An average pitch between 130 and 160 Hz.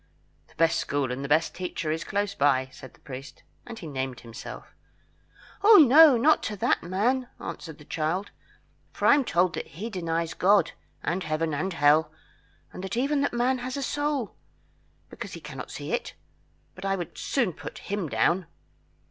No: medium, 185 Hz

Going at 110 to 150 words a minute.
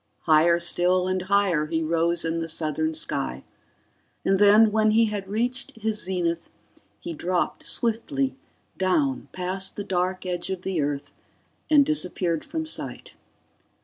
Yes: average, 145 wpm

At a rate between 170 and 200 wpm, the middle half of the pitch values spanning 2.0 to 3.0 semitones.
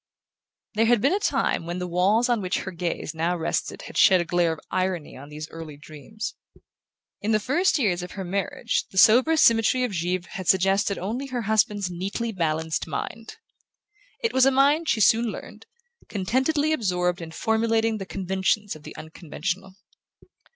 No: average, 175 wpm; average, 4.4 semitones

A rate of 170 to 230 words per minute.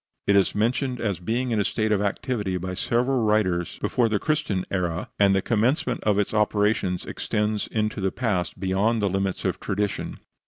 Yes: average, 185 wpm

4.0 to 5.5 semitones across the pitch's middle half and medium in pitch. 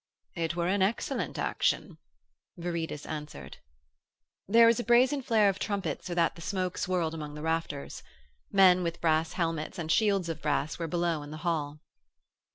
No: average, 3.3 semitones; medium, 170 Hz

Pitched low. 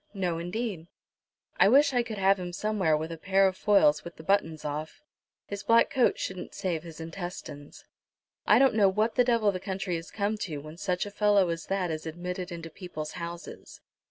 No: medium, 185 Hz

